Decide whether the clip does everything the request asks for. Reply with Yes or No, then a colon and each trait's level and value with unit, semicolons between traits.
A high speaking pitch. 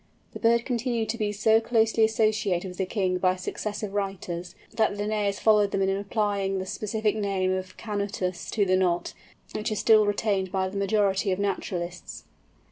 Yes: high, 200 Hz